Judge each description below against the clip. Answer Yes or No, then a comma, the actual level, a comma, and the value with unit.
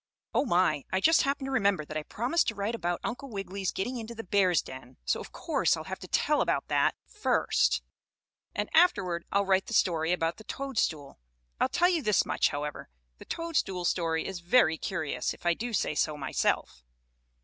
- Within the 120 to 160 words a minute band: No, average, 195 wpm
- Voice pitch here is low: No, high, 190 Hz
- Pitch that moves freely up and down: Yes, wide, 6.2 semitones